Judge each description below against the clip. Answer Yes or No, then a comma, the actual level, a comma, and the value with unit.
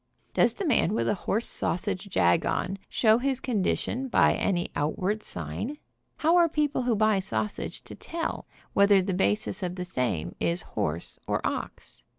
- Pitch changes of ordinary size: No, wide, 5.8 semitones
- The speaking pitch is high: Yes, high, 200 Hz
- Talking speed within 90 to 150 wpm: No, average, 170 wpm